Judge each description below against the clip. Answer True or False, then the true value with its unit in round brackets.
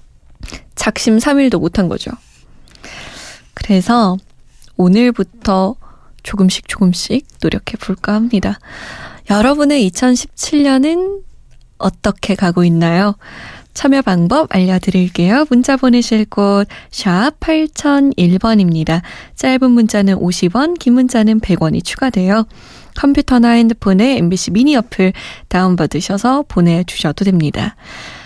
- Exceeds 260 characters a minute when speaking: False (230 characters per minute)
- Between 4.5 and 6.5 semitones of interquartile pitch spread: True (5.6 semitones)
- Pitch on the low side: False (215 Hz)